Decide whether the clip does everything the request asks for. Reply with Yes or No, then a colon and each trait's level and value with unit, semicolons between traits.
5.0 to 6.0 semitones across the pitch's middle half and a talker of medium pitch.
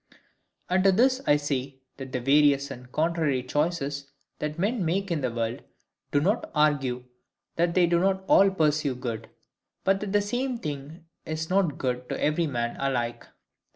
Yes: wide, 5.4 semitones; medium, 150 Hz